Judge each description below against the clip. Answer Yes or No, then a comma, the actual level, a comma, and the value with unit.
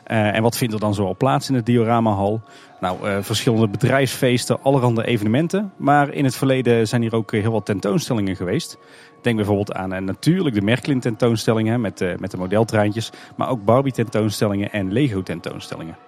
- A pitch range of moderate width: Yes, average, 3.6 semitones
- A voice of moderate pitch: No, low, 115 Hz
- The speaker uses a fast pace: No, average, 170 wpm